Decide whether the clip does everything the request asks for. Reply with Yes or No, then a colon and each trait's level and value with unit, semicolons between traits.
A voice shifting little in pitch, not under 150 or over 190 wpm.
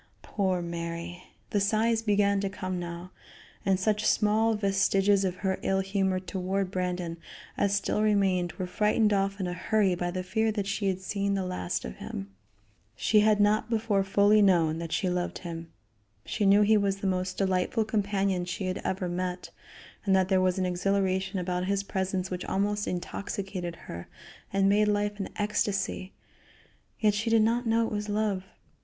Yes: narrow, 2.1 semitones; average, 180 wpm